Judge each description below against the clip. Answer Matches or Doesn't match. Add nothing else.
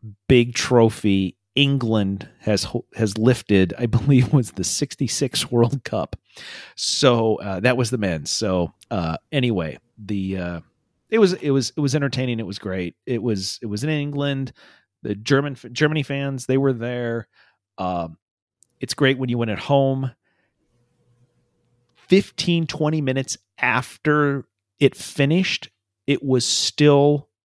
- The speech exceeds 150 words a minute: Doesn't match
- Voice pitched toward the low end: Matches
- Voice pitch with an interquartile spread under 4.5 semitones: Doesn't match